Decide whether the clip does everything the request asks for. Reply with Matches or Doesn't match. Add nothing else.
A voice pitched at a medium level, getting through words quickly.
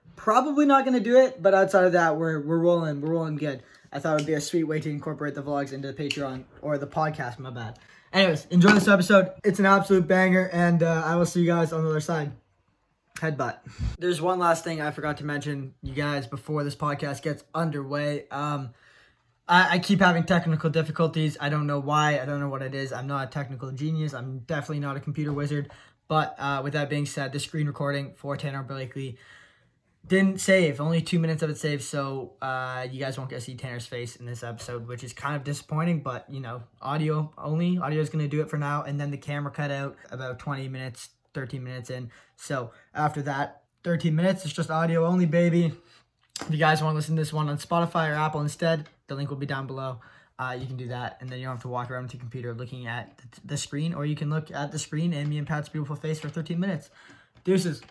Matches